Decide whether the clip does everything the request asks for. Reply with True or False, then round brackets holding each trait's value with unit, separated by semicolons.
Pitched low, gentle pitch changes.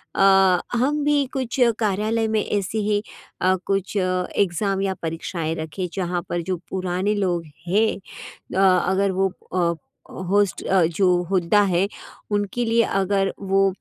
False (195 Hz; 2.1 semitones)